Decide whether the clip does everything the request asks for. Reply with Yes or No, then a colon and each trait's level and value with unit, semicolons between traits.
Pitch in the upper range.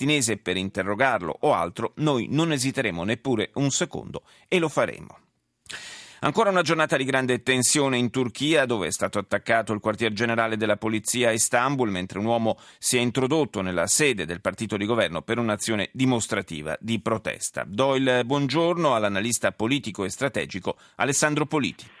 No: low, 120 Hz